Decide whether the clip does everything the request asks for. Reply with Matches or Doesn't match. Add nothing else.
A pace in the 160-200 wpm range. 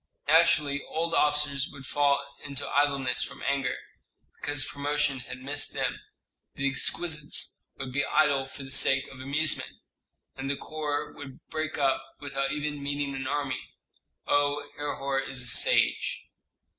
Doesn't match